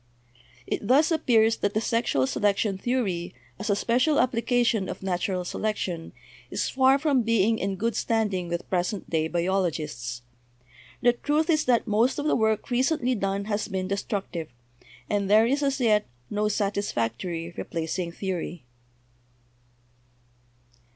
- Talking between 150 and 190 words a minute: No, average, 140 wpm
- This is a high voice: Yes, high, 205 Hz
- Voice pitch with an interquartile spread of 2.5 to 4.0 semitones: No, average, 4.8 semitones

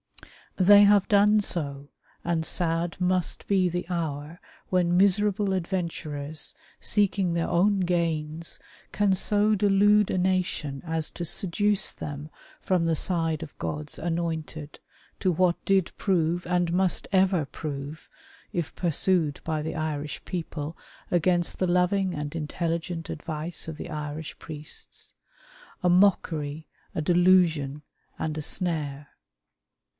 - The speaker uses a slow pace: Yes, slow, 130 wpm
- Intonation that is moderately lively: Yes, average, 3.1 semitones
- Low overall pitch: No, medium, 170 Hz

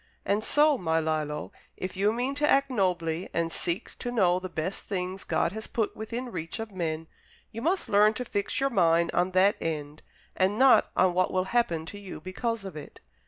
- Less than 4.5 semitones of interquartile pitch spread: No, average, 5.1 semitones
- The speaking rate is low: No, fast, 205 wpm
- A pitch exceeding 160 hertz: Yes, high, 190 Hz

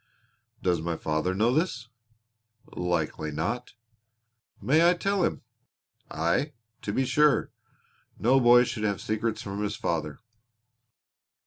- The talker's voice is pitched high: No, low, 110 Hz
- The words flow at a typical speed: No, slow, 120 wpm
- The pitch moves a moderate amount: No, wide, 7.4 semitones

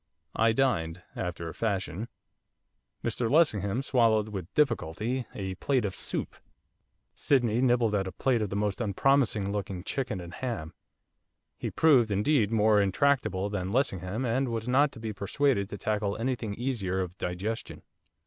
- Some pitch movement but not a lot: Yes, average, 4.4 semitones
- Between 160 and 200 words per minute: No, average, 150 wpm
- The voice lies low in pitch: Yes, low, 110 Hz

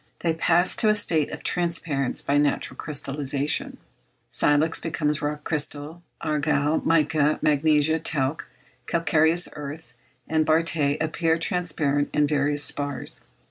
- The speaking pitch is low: No, medium, 150 Hz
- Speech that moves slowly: Yes, slow, 120 wpm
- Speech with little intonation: Yes, narrow, 1.9 semitones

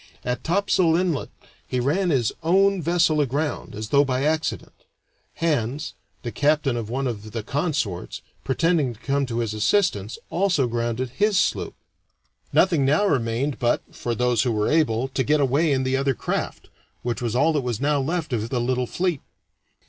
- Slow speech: No, average, 175 wpm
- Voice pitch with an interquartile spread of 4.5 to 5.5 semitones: Yes, average, 4.9 semitones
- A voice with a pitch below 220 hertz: Yes, low, 135 Hz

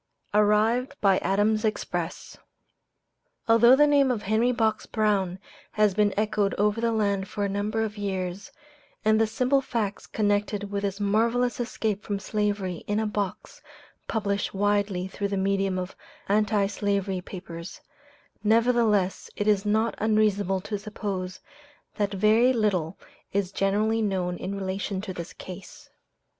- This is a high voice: Yes, high, 205 Hz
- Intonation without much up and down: Yes, narrow, 1.9 semitones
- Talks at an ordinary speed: Yes, average, 145 wpm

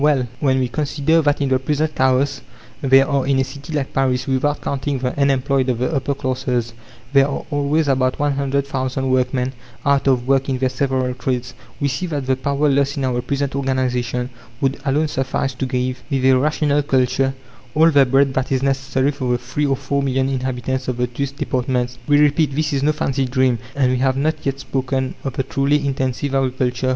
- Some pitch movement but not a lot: No, narrow, 1.5 semitones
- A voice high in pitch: No, low, 135 Hz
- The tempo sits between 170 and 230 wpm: Yes, fast, 205 wpm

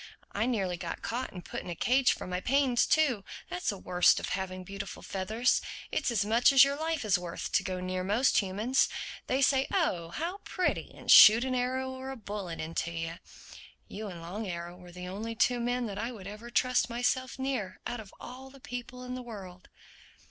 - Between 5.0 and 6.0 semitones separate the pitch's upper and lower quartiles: Yes, wide, 5.5 semitones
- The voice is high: Yes, high, 225 Hz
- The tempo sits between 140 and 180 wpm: No, fast, 205 wpm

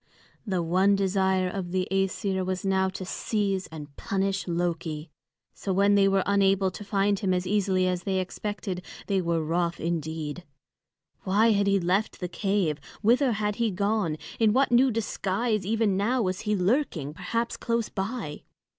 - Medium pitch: No, high, 195 Hz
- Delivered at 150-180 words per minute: Yes, average, 165 wpm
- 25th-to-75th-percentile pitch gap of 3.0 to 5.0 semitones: No, narrow, 2.5 semitones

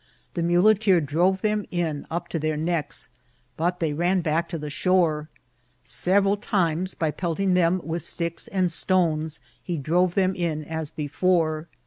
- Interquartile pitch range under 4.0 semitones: Yes, average, 2.7 semitones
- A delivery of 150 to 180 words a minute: Yes, average, 160 wpm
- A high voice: No, medium, 170 Hz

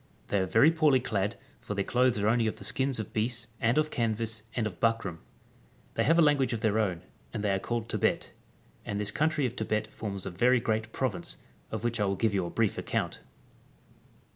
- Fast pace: Yes, fast, 220 wpm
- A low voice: Yes, low, 110 Hz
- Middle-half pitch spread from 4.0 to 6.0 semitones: No, average, 3.2 semitones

